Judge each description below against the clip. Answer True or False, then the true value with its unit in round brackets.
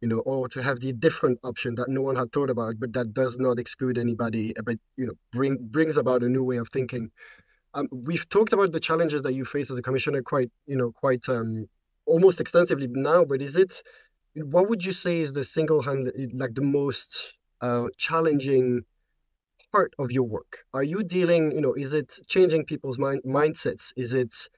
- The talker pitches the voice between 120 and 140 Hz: True (135 Hz)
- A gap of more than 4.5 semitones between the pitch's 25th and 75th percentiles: False (3.5 semitones)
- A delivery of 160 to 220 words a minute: True (205 wpm)